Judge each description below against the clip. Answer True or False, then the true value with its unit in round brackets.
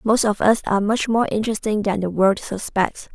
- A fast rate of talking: True (210 wpm)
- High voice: True (210 Hz)